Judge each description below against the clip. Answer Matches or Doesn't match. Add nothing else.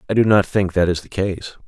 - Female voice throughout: Doesn't match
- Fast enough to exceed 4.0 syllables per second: Matches